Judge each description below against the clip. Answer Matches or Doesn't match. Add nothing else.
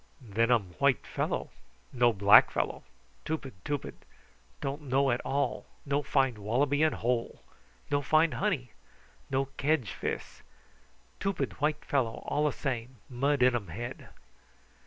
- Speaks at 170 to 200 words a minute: Doesn't match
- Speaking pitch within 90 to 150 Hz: Matches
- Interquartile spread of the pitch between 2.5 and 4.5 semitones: Matches